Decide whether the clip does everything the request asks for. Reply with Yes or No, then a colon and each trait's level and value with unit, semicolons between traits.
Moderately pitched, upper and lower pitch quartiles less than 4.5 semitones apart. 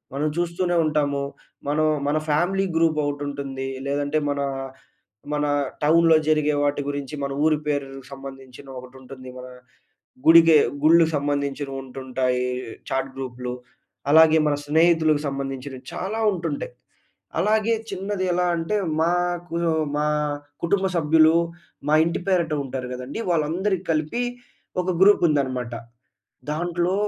Yes: medium, 150 Hz; average, 3.7 semitones